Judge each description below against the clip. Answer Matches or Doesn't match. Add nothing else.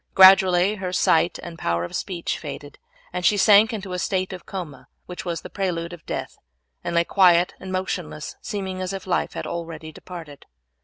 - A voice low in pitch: Doesn't match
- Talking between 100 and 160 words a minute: Doesn't match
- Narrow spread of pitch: Matches